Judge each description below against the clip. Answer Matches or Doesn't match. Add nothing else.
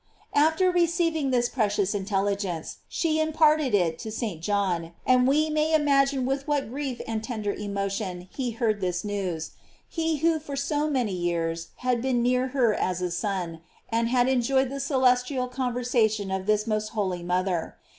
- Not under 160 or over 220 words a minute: Matches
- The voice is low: Doesn't match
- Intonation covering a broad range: Matches